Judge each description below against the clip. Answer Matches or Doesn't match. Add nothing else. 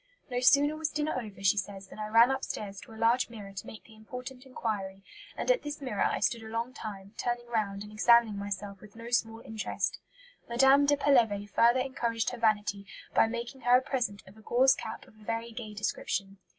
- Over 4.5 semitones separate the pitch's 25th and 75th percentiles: Doesn't match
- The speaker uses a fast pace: Matches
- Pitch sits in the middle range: Doesn't match